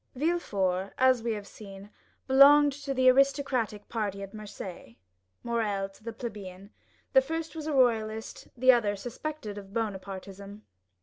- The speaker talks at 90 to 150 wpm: Yes, average, 140 wpm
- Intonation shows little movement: No, average, 4.8 semitones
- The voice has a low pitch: No, high, 220 Hz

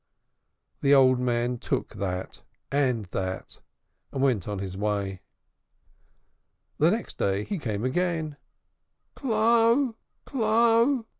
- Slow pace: Yes, slow, 105 wpm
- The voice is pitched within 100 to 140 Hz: Yes, low, 135 Hz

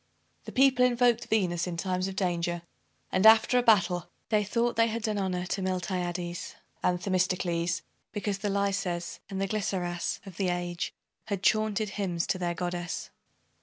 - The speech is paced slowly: No, average, 165 wpm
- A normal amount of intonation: Yes, average, 3.1 semitones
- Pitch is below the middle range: No, high, 190 Hz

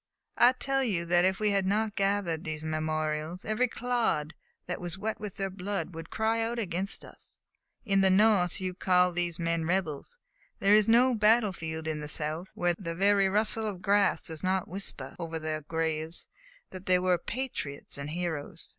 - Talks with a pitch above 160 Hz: Yes, medium, 185 Hz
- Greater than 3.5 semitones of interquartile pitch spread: Yes, average, 4.3 semitones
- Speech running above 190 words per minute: No, average, 185 wpm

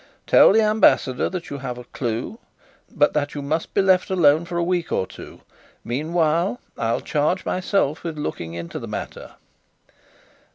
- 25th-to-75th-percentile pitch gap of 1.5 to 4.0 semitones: No, average, 5.1 semitones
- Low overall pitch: No, medium, 155 Hz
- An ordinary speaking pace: Yes, average, 165 wpm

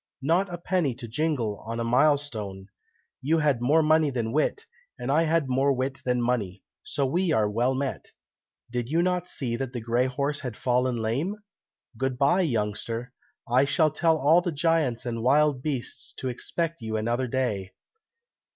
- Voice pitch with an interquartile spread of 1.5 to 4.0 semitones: No, average, 4.6 semitones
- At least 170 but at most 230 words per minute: Yes, average, 180 wpm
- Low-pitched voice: Yes, low, 130 Hz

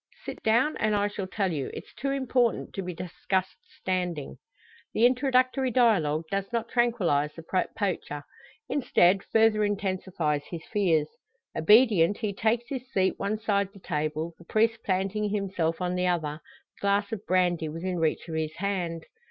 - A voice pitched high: Yes, high, 195 Hz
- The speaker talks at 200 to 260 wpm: No, average, 160 wpm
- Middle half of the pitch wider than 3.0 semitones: Yes, average, 4.6 semitones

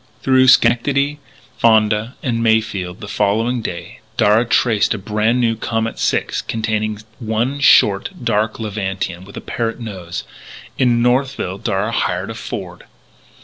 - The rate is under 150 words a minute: Yes, slow, 135 wpm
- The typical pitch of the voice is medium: No, low, 110 Hz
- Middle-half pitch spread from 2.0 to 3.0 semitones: Yes, narrow, 2.5 semitones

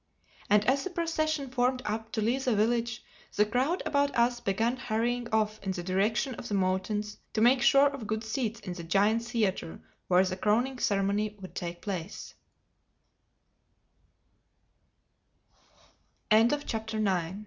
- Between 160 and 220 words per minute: No, slow, 135 wpm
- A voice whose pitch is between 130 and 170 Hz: No, high, 220 Hz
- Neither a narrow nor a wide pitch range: Yes, average, 3.6 semitones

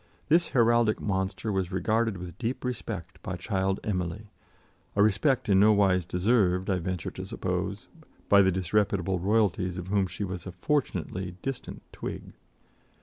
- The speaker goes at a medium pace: Yes, average, 150 wpm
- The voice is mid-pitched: No, very low, 95 Hz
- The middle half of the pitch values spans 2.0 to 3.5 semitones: Yes, average, 2.9 semitones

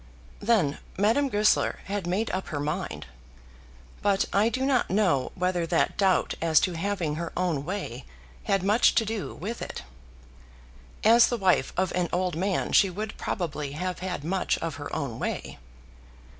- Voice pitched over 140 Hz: Yes, medium, 185 Hz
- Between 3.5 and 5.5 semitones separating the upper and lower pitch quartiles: Yes, average, 3.8 semitones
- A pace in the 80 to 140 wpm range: No, average, 165 wpm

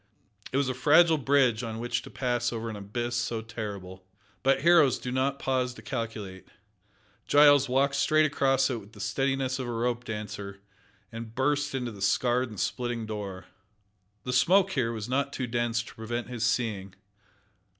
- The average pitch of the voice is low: Yes, low, 120 Hz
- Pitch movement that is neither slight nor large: Yes, average, 3.3 semitones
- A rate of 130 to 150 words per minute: No, average, 175 wpm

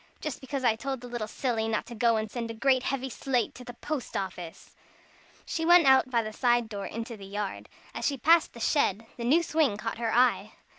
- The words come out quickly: Yes, fast, 230 wpm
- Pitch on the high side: Yes, high, 240 Hz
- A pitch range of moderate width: Yes, average, 3.3 semitones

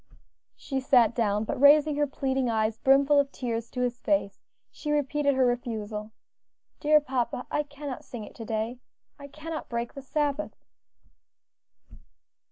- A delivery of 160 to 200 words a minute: No, average, 150 wpm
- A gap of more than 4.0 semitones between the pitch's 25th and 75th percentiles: No, average, 3.7 semitones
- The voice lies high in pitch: Yes, very high, 265 Hz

